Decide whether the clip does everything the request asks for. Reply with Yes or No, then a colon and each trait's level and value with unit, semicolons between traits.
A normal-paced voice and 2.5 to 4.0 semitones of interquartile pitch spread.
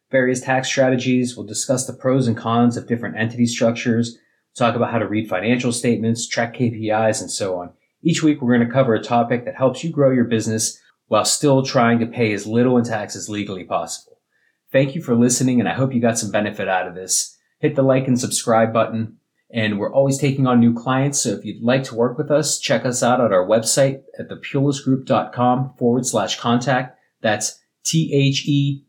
No: fast, 210 wpm; average, 2.8 semitones